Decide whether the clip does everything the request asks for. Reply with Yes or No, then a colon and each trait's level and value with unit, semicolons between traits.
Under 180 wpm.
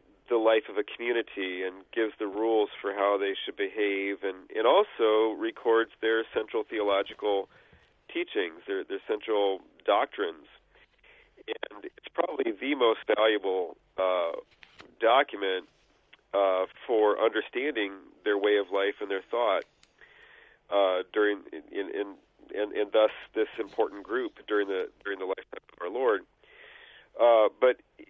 Yes: average, 140 wpm